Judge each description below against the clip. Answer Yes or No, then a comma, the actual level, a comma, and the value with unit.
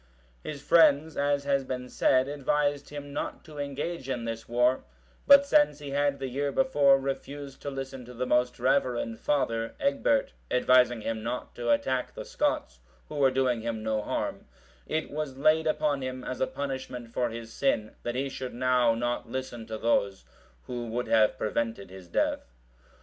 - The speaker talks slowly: No, average, 180 wpm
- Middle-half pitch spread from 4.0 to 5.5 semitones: No, average, 3.1 semitones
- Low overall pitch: Yes, low, 130 Hz